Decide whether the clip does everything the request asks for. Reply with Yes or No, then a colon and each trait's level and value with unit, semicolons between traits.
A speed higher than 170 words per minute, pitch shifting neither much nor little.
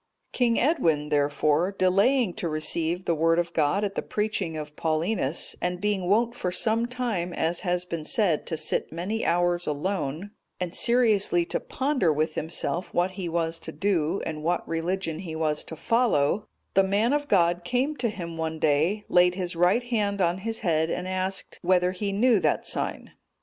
Yes: average, 180 wpm; average, 4.0 semitones